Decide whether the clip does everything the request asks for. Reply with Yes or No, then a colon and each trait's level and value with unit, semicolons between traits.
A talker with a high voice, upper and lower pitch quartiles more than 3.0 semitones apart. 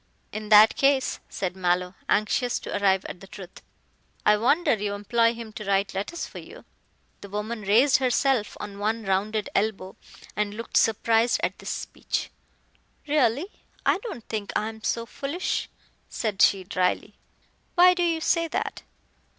Yes: high, 215 Hz; average, 3.6 semitones